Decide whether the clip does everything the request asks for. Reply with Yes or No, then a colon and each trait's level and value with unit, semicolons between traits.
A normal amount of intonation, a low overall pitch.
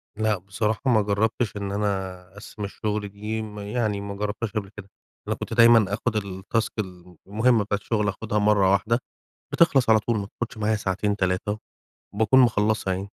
No: narrow, 1.7 semitones; low, 105 Hz